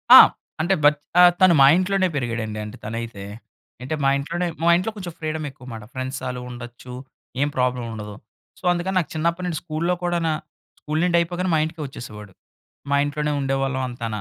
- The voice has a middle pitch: Yes, medium, 145 Hz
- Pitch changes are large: Yes, wide, 5.8 semitones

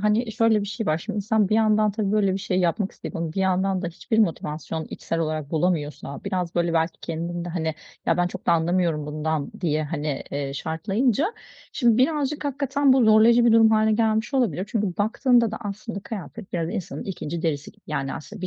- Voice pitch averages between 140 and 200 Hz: Yes, high, 190 Hz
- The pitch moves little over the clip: No, average, 5.1 semitones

